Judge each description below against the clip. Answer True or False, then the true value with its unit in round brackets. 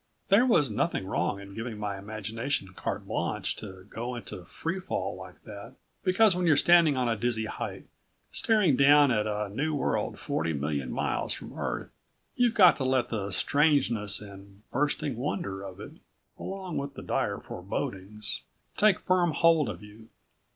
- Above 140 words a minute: True (165 wpm)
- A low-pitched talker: True (120 Hz)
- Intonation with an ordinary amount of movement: False (7.6 semitones)